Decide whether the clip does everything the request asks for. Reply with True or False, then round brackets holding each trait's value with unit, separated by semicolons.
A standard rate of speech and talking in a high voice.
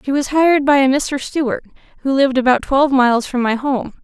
False (225 wpm; 265 Hz)